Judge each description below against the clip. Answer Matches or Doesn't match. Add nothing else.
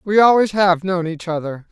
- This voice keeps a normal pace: Doesn't match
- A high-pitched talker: Doesn't match